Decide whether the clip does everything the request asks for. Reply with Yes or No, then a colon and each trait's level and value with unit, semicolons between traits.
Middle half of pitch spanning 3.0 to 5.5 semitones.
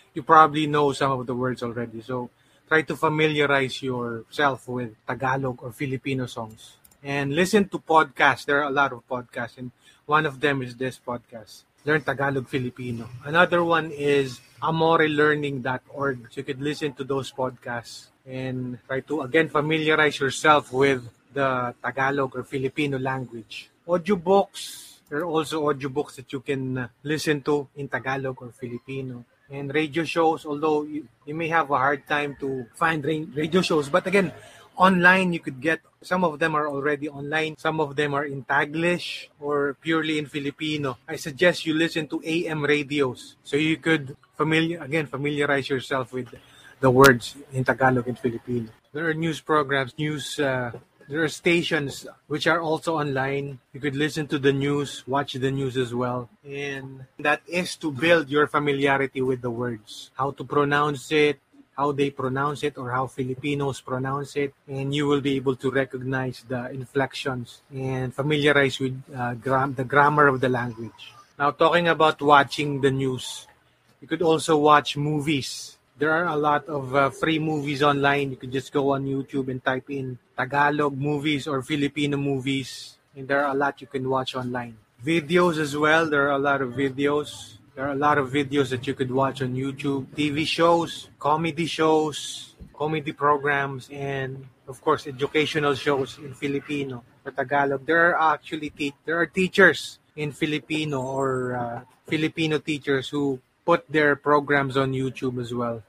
No: narrow, 2.5 semitones